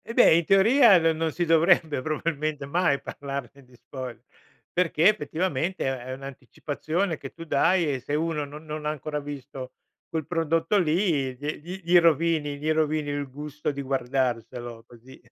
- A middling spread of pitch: Yes, average, 3.3 semitones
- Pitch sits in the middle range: Yes, medium, 150 Hz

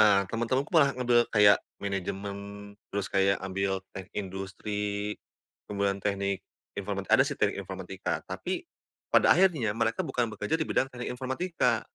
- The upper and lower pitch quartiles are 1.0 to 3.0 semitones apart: No, average, 3.8 semitones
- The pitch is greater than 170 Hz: No, low, 105 Hz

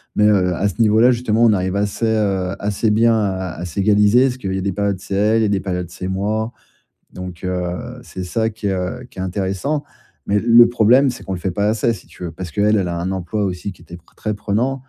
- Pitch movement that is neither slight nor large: Yes, average, 3.2 semitones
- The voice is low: Yes, low, 100 Hz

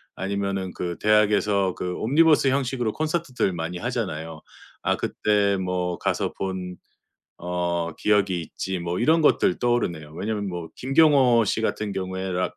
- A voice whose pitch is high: No, very low, 95 Hz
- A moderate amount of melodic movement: Yes, average, 4.6 semitones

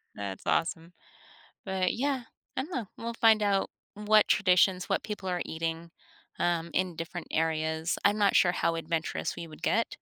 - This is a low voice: No, medium, 180 Hz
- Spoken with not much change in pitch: No, average, 4.0 semitones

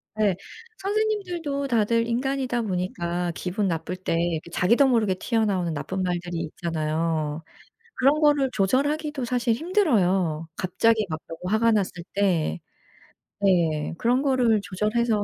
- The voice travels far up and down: Yes, wide, 6.6 semitones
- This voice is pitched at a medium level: No, high, 205 Hz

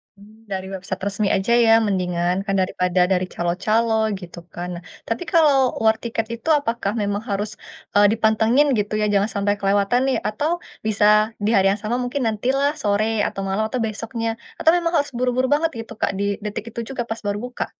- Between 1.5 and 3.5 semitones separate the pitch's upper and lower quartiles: Yes, average, 3.0 semitones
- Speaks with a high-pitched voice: Yes, high, 215 Hz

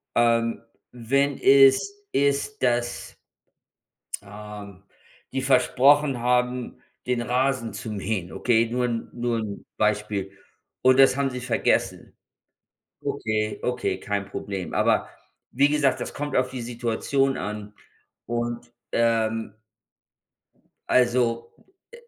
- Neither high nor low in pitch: No, low, 120 Hz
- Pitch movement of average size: Yes, average, 3.1 semitones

